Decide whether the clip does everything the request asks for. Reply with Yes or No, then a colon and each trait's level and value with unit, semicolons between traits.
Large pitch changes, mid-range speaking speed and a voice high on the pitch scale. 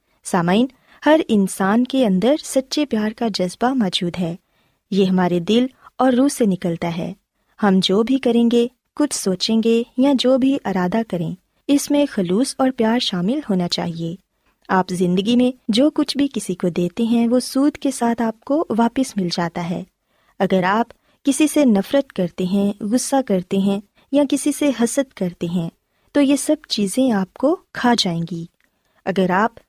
Yes: wide, 6.0 semitones; average, 175 wpm; high, 230 Hz